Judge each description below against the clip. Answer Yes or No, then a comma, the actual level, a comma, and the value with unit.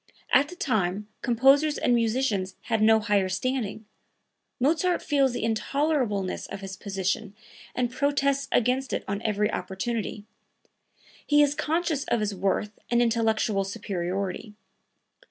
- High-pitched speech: Yes, high, 225 Hz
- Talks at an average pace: No, slow, 130 wpm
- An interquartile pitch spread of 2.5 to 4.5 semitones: No, average, 5.1 semitones